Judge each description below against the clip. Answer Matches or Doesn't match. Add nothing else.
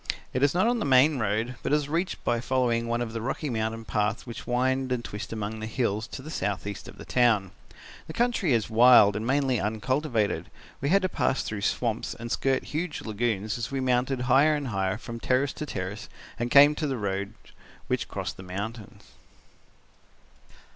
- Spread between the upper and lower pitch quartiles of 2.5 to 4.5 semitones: Matches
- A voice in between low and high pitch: Doesn't match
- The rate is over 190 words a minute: Matches